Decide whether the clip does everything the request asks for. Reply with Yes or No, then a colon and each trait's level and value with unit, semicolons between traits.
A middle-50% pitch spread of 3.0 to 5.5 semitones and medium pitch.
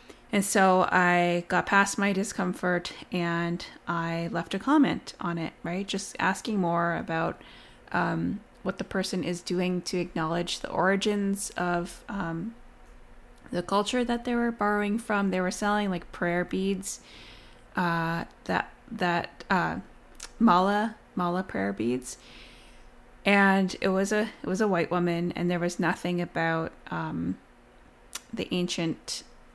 No: narrow, 2.6 semitones; medium, 180 Hz